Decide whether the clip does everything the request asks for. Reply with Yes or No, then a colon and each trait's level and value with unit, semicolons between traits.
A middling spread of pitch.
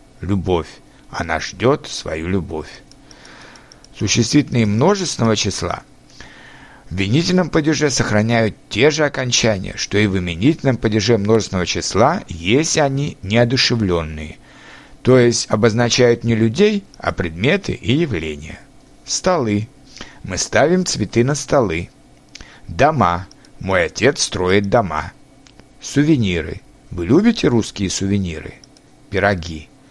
No: wide, 6.2 semitones